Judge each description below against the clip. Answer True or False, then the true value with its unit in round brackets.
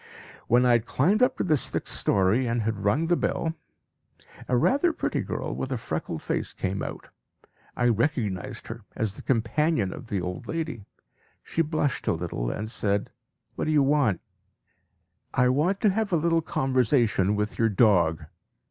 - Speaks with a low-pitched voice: True (120 Hz)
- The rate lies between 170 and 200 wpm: True (175 wpm)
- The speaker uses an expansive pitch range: True (7.1 semitones)